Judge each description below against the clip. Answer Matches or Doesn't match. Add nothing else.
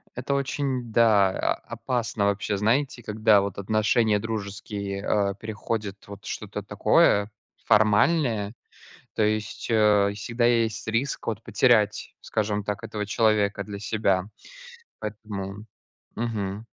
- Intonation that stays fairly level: Matches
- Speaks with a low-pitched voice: Matches